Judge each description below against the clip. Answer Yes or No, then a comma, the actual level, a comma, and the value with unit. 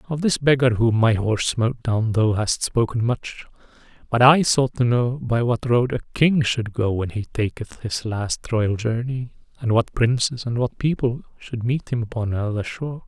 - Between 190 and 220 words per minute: Yes, average, 195 wpm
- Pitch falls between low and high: No, low, 120 Hz